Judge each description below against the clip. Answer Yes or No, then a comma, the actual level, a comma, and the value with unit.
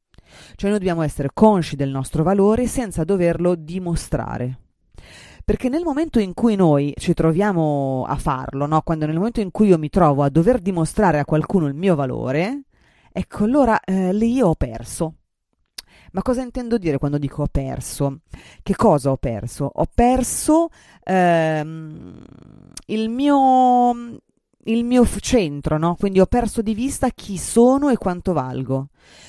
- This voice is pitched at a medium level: Yes, medium, 180 Hz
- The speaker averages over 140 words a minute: Yes, average, 155 wpm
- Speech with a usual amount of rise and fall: No, wide, 7.6 semitones